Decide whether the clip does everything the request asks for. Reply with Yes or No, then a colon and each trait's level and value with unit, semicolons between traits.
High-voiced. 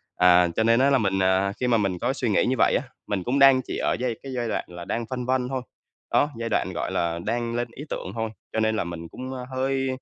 No: low, 115 Hz